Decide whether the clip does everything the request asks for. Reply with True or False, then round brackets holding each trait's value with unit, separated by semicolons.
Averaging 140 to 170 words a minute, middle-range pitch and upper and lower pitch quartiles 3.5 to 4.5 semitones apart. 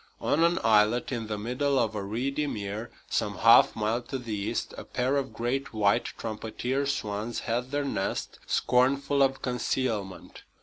False (165 wpm; 120 Hz; 4.0 semitones)